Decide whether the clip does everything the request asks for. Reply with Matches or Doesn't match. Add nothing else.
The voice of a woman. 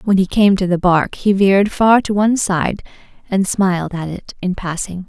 Matches